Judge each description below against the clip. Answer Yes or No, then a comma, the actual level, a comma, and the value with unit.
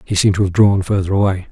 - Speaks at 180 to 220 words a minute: No, fast, 275 wpm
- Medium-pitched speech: No, very low, 95 Hz